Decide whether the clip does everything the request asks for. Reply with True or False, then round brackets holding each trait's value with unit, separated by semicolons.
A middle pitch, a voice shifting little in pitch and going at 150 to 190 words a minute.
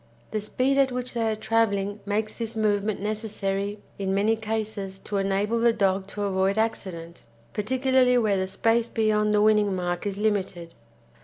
False (210 Hz; 2.2 semitones; 165 wpm)